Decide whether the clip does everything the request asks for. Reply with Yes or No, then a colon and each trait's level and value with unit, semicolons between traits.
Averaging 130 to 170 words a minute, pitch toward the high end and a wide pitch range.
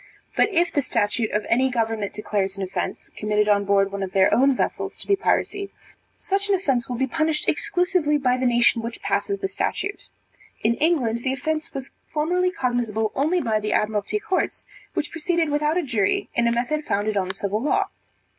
No: average, 195 wpm; very high, 250 Hz; wide, 6.9 semitones